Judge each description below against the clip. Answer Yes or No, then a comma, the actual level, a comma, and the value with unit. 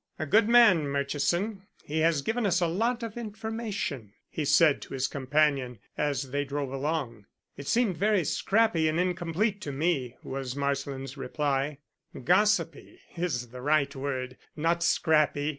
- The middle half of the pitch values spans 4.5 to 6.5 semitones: Yes, average, 5.2 semitones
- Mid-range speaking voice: Yes, medium, 155 Hz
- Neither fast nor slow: Yes, average, 150 wpm